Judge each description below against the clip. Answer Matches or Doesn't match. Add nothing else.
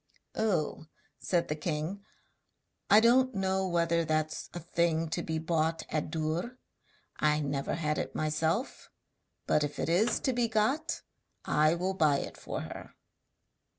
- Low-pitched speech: Doesn't match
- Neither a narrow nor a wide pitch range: Matches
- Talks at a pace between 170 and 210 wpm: Doesn't match